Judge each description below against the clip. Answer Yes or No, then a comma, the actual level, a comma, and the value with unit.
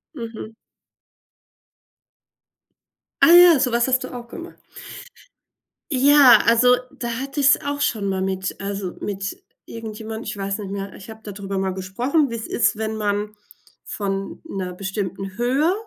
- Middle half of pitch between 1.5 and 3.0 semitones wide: No, average, 4.2 semitones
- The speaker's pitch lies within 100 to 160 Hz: No, high, 220 Hz